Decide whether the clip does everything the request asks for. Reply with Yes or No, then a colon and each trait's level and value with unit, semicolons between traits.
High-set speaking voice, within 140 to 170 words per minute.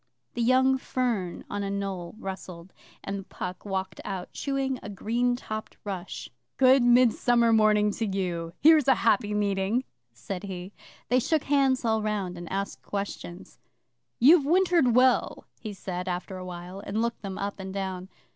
Yes: high, 205 Hz; average, 160 wpm